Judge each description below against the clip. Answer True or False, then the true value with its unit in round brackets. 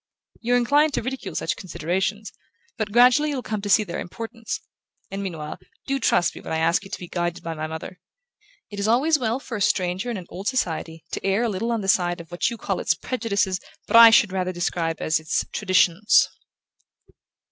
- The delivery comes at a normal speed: False (210 wpm)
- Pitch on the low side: False (200 Hz)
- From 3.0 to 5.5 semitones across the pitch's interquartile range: True (4.9 semitones)